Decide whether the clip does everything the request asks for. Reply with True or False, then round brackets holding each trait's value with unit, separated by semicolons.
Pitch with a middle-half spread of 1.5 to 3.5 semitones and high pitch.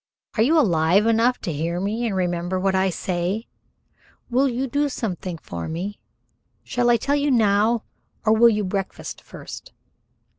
False (4.6 semitones; 205 Hz)